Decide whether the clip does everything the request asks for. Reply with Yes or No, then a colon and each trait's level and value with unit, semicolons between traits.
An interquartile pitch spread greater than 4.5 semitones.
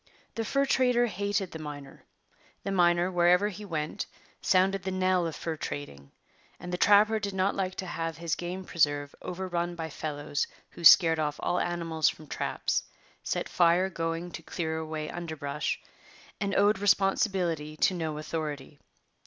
No: average, 3.3 semitones